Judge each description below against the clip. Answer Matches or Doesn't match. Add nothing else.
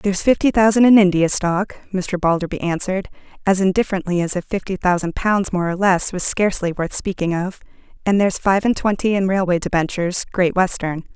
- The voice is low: Doesn't match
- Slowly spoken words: Doesn't match